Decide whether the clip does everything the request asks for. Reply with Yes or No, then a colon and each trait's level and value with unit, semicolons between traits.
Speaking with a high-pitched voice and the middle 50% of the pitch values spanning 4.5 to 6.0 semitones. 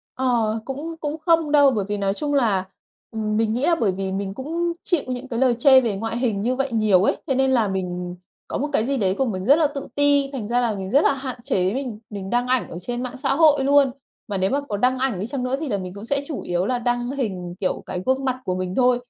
Yes: high, 245 Hz; average, 5.2 semitones